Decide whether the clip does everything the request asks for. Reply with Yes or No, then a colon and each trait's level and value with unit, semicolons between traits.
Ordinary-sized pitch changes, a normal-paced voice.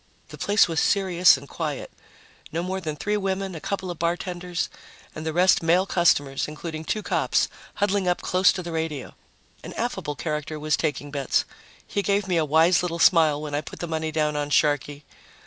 Yes: average, 3.3 semitones; average, 195 wpm